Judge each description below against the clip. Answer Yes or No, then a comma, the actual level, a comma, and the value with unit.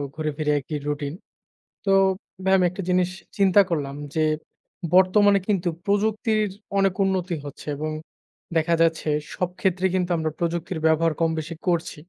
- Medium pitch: Yes, medium, 175 Hz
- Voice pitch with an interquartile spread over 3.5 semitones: No, average, 3.2 semitones